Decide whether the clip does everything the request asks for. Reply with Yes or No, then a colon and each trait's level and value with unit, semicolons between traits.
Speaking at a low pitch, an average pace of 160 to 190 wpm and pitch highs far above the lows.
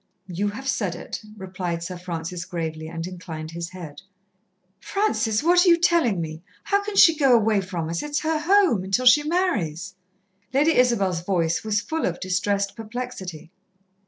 No: high, 195 Hz; average, 165 wpm; wide, 8.6 semitones